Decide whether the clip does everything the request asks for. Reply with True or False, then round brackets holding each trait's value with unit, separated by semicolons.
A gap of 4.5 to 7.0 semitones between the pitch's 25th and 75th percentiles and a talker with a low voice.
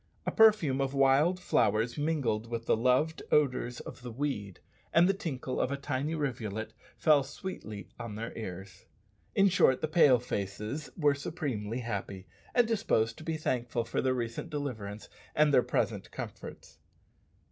True (5.1 semitones; 130 Hz)